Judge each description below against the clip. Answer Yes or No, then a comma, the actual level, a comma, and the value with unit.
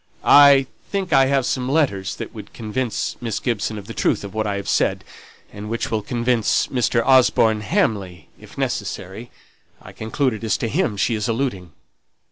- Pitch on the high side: No, low, 115 Hz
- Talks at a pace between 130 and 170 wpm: No, average, 180 wpm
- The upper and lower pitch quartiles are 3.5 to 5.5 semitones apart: Yes, average, 3.9 semitones